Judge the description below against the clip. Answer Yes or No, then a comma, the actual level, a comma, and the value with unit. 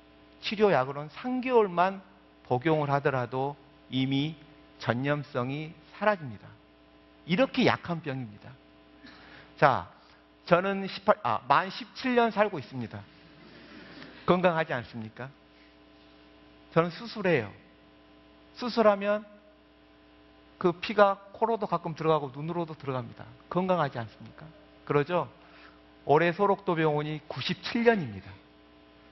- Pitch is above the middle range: No, medium, 140 Hz